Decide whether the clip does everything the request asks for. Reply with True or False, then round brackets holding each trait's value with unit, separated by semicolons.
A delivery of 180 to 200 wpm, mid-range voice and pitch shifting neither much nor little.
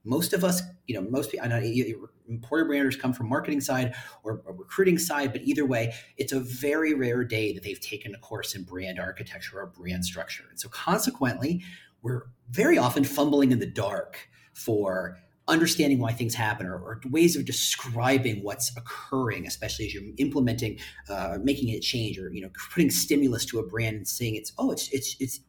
False (195 wpm; 125 Hz; 4.2 semitones)